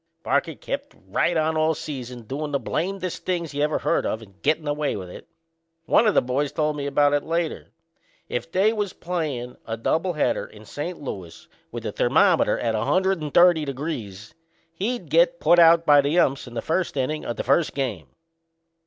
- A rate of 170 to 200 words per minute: Yes, average, 190 wpm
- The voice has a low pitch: No, medium, 150 Hz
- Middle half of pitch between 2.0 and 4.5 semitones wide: No, average, 4.9 semitones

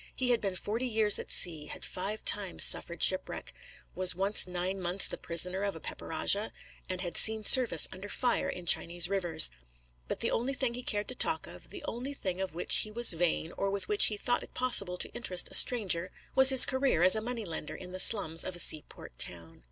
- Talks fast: Yes, fast, 220 wpm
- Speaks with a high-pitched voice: Yes, high, 195 Hz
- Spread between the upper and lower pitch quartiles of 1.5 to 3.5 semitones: No, average, 4.7 semitones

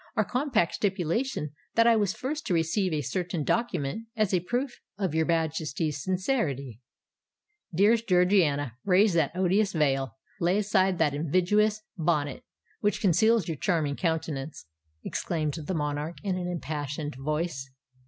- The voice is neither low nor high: Yes, medium, 175 Hz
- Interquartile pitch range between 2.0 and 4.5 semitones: No, average, 5.3 semitones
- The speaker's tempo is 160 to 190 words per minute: No, slow, 135 wpm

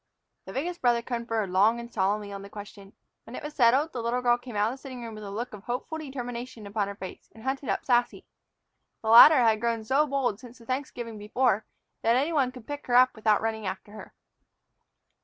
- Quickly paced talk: Yes, fast, 225 wpm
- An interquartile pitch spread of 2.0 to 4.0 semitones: Yes, average, 3.1 semitones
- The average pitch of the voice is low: No, high, 235 Hz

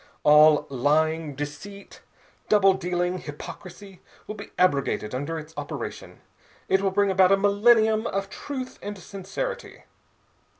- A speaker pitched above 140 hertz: Yes, high, 190 Hz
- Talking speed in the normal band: No, slow, 125 wpm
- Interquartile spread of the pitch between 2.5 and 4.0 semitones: No, average, 4.7 semitones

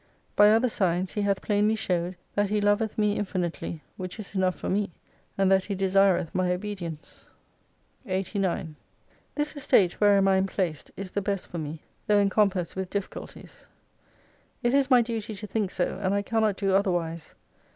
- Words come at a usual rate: Yes, average, 175 wpm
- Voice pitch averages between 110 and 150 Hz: No, high, 195 Hz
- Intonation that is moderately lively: No, narrow, 2.2 semitones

